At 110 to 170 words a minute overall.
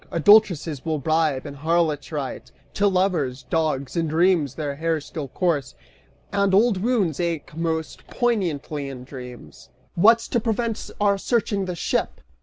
Yes: average, 150 wpm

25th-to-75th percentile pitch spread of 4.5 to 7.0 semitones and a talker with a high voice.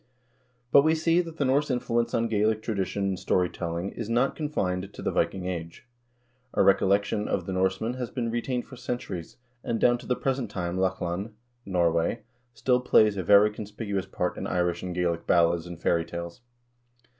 No: average, 4.9 semitones; low, 100 Hz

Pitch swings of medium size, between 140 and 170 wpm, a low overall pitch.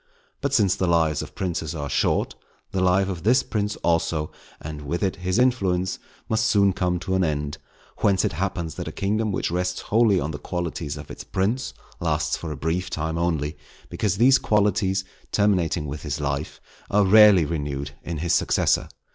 No: average, 4.1 semitones; average, 185 wpm; very low, 90 Hz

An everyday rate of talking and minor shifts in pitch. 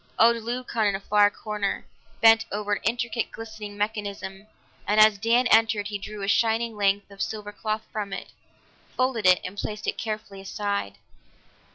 Yes: average, 170 wpm; narrow, 1.8 semitones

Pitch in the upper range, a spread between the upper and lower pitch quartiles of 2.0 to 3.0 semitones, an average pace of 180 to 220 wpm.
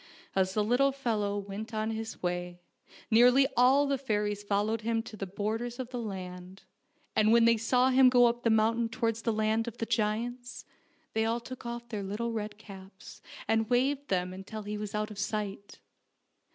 Yes: high, 220 Hz; narrow, 2.5 semitones; average, 190 wpm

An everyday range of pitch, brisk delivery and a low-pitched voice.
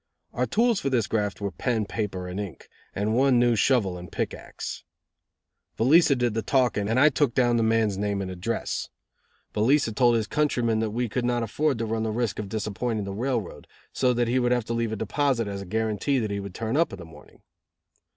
Yes: average, 3.2 semitones; fast, 220 wpm; low, 115 Hz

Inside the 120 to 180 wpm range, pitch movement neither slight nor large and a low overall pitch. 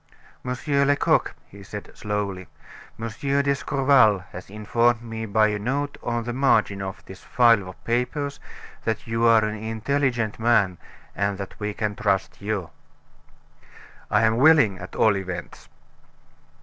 Yes: average, 140 wpm; average, 3.5 semitones; low, 110 Hz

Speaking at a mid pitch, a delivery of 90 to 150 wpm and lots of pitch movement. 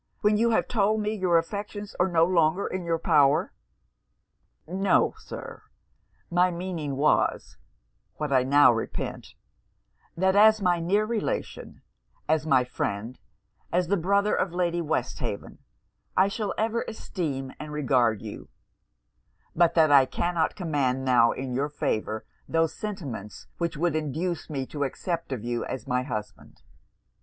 Yes: medium, 165 Hz; average, 145 wpm; wide, 5.7 semitones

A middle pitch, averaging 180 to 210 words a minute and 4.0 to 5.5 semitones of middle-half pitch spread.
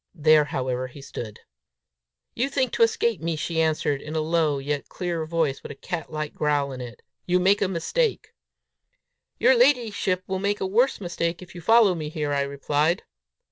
Yes: medium, 165 Hz; average, 185 wpm; average, 4.6 semitones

